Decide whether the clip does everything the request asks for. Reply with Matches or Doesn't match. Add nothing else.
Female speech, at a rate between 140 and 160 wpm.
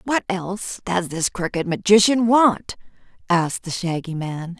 Matches